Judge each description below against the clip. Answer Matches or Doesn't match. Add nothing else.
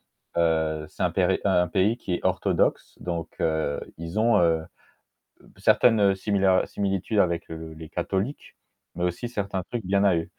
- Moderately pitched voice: Doesn't match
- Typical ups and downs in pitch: Matches